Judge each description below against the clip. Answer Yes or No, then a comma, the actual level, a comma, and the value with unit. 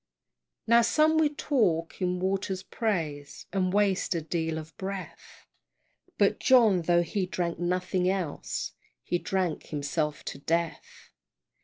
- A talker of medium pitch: Yes, medium, 180 Hz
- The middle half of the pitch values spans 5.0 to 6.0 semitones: No, average, 3.1 semitones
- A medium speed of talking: No, slow, 130 wpm